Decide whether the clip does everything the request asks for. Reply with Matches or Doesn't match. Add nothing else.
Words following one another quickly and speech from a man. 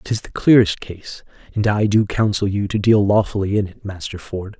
Matches